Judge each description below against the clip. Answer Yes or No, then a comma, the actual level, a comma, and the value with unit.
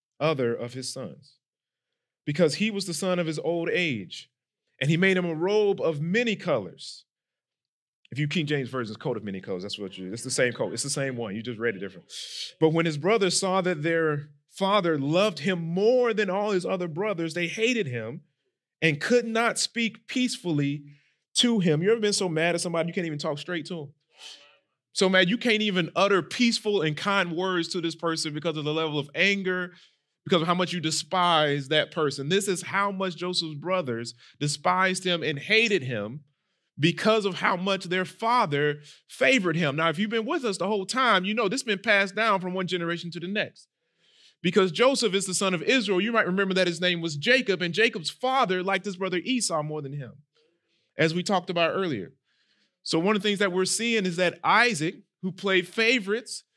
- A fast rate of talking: Yes, fast, 210 wpm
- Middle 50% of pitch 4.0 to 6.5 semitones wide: Yes, average, 4.3 semitones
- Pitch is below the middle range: No, medium, 180 Hz